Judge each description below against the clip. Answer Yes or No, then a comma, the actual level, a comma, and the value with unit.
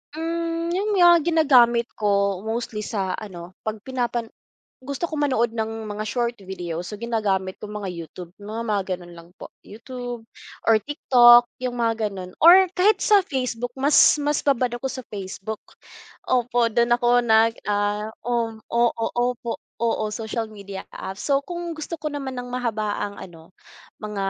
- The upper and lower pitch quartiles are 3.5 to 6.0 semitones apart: Yes, average, 3.9 semitones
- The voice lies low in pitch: No, high, 235 Hz